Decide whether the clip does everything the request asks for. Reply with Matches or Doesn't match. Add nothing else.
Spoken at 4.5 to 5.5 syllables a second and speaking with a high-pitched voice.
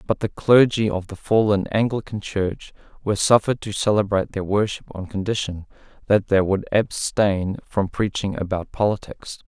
Doesn't match